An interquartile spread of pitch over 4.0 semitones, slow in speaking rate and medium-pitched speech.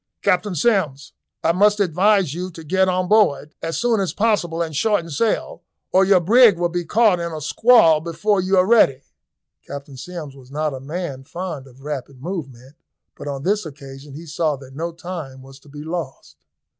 No: average, 5.1 semitones; average, 190 wpm; medium, 165 Hz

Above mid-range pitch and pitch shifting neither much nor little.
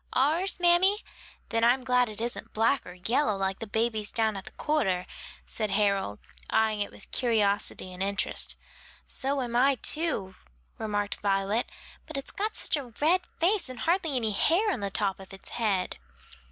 No: high, 225 Hz; wide, 5.8 semitones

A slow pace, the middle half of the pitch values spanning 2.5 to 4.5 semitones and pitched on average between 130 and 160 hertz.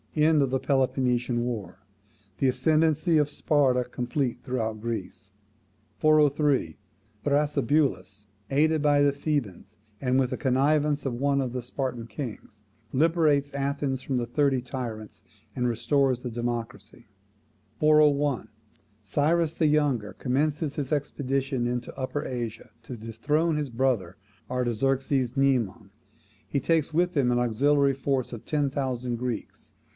Yes: slow, 130 wpm; average, 3.3 semitones; low, 135 Hz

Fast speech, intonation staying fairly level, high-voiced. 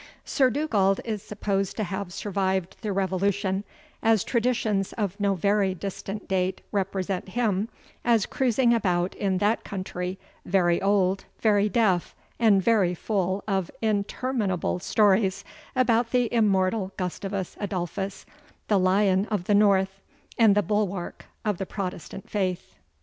No: slow, 135 wpm; narrow, 2.2 semitones; high, 195 Hz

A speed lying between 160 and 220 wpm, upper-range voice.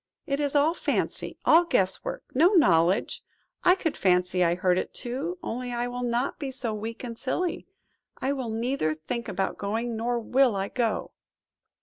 Yes: average, 180 wpm; high, 240 Hz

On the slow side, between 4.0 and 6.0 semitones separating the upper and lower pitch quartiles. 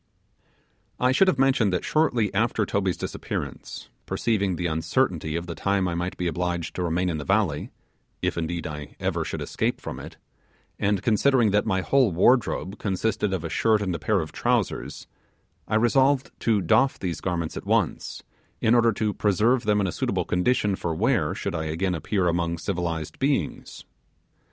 No: average, 180 wpm; average, 4.6 semitones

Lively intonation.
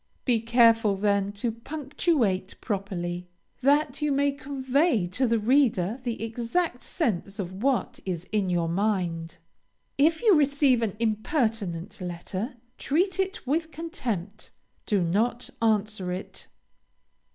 Yes: wide, 6.1 semitones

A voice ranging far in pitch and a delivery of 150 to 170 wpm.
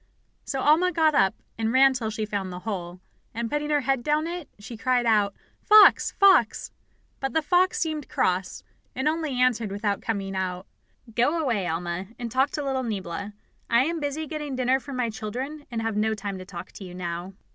No: wide, 6.6 semitones; average, 200 wpm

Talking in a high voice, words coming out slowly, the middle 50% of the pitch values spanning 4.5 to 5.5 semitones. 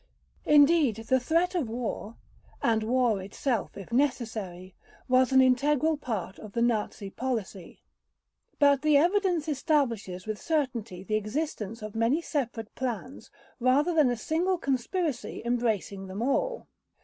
Yes: very high, 250 Hz; slow, 125 wpm; average, 5.2 semitones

